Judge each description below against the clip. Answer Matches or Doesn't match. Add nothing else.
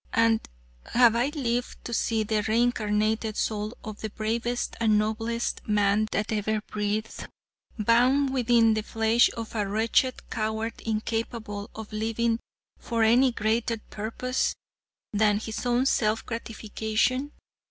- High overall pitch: Matches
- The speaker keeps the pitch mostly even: Matches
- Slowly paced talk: Matches